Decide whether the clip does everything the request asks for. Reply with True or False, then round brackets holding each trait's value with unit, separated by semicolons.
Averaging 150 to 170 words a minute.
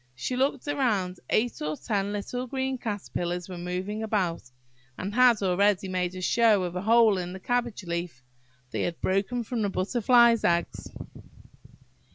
True (155 wpm)